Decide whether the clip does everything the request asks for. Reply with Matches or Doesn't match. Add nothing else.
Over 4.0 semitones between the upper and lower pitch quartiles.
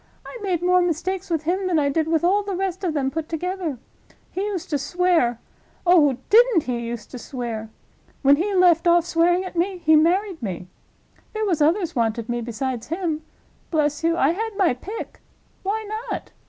Matches